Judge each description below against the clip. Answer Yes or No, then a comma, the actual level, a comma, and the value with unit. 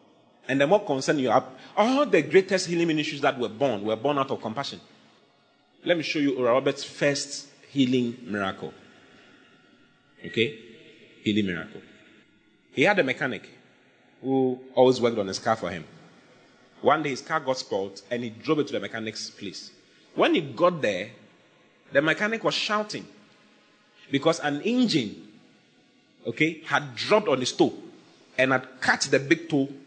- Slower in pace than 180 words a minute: Yes, average, 160 wpm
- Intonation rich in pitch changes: No, average, 4.8 semitones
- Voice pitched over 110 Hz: Yes, medium, 140 Hz